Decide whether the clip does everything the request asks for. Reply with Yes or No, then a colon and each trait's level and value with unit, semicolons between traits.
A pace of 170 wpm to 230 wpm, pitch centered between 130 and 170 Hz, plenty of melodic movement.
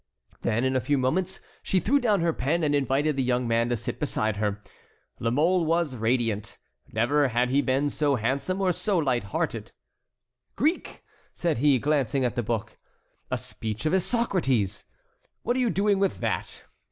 Yes: average, 175 wpm; medium, 140 Hz; wide, 6.3 semitones